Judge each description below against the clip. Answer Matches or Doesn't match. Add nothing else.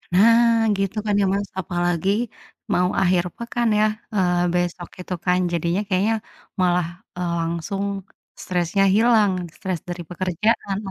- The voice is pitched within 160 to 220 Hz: Matches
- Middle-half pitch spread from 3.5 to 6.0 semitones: Doesn't match